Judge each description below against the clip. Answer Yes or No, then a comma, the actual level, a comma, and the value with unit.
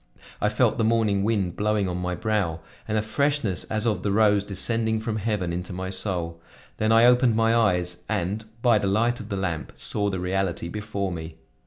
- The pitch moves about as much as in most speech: Yes, average, 3.3 semitones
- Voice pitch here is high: No, low, 105 Hz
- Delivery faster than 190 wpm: Yes, average, 200 wpm